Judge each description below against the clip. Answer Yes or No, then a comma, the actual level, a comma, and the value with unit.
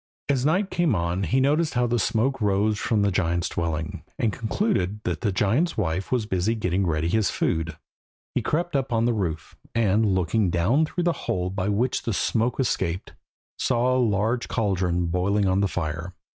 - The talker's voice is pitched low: Yes, low, 105 Hz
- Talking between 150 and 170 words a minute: No, average, 190 wpm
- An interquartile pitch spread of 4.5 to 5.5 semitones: Yes, average, 5.1 semitones